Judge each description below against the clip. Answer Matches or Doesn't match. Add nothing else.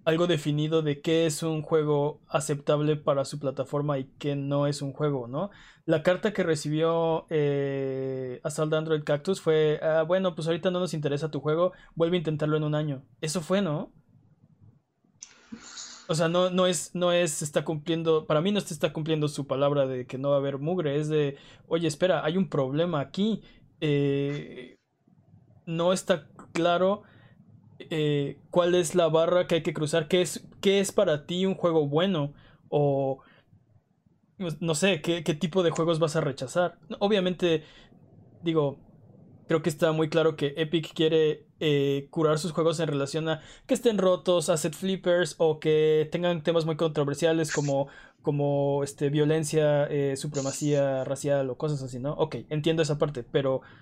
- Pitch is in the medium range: Matches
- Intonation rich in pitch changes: Doesn't match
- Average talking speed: Matches